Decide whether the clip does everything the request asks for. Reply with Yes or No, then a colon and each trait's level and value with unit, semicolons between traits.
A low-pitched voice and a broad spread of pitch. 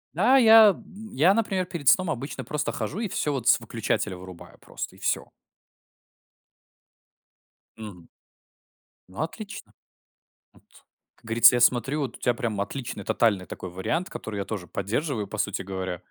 Yes: low, 120 Hz; wide, 8.8 semitones